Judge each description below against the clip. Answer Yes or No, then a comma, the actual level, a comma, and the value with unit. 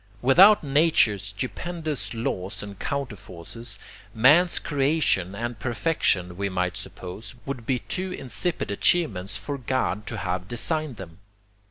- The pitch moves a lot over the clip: Yes, wide, 6.8 semitones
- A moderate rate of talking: No, slow, 125 wpm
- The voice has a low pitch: Yes, low, 120 Hz